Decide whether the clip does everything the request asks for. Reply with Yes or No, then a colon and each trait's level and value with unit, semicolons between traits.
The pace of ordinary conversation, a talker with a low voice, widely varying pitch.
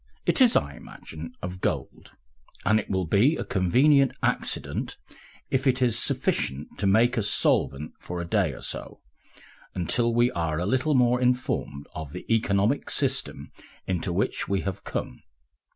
Yes: average, 160 wpm; low, 100 Hz; wide, 6.3 semitones